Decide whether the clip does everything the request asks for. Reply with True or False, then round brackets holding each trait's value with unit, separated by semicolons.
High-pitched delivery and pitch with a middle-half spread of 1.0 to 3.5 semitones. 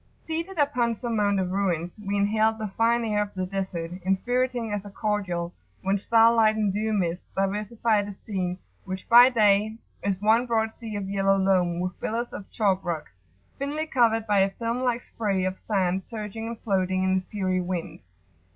True (205 Hz; 3.1 semitones)